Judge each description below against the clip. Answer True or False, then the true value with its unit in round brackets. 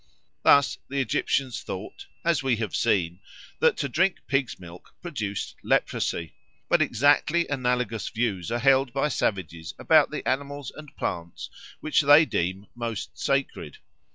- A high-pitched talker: False (125 Hz)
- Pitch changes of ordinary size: False (5.7 semitones)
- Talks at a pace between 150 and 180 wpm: False (140 wpm)